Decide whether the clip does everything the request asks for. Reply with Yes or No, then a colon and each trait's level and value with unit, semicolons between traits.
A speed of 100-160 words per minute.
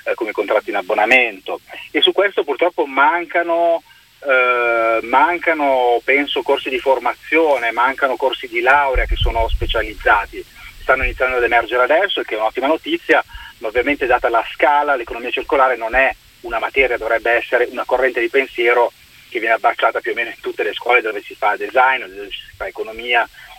No: fast, 170 wpm